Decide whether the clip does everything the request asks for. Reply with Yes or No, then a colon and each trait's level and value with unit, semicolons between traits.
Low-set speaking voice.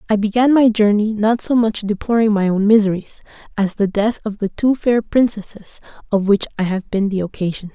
No: high, 210 Hz